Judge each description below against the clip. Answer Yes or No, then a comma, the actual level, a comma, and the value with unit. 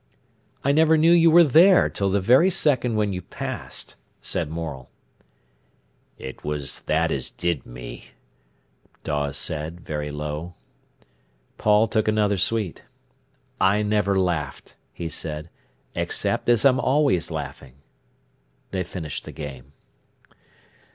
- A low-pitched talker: Yes, very low, 95 Hz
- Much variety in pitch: Yes, wide, 7.7 semitones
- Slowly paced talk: Yes, slow, 125 wpm